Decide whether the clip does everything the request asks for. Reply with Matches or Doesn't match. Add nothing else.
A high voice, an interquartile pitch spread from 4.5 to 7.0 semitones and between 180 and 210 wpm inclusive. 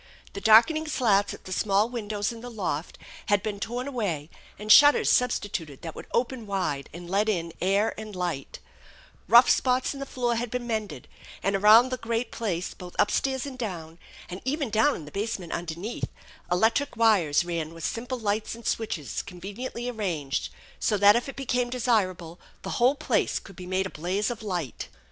Matches